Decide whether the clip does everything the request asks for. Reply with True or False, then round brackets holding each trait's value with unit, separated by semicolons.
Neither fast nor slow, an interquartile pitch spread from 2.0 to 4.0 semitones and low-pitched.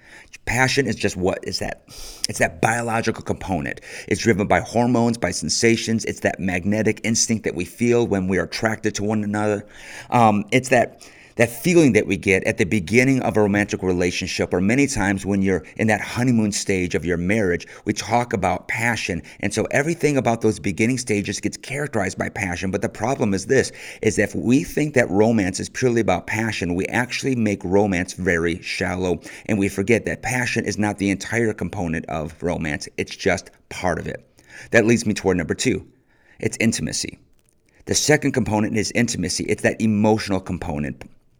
True (185 wpm; 3.5 semitones; 105 Hz)